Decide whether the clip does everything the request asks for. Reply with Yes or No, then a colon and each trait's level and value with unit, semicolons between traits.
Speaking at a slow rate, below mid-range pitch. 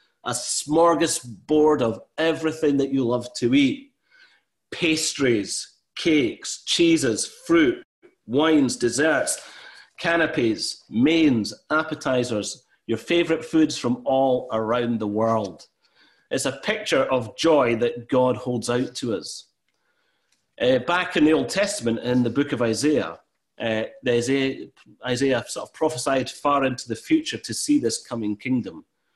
No: slow, 130 wpm; medium, 145 Hz